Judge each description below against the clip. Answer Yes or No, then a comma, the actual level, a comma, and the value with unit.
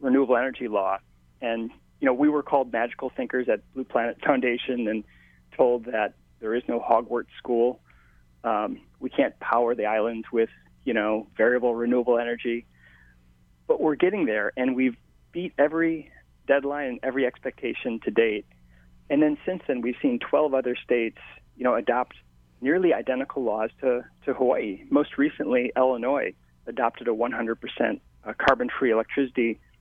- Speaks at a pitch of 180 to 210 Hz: No, low, 120 Hz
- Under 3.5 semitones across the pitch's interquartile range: No, average, 5.3 semitones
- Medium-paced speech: Yes, average, 155 wpm